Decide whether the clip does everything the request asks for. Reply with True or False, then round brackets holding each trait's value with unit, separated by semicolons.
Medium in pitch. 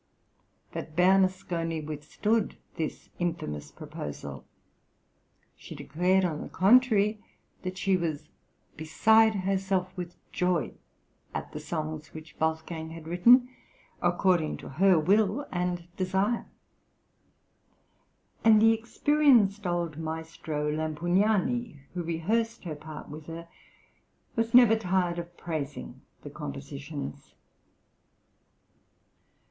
True (175 Hz)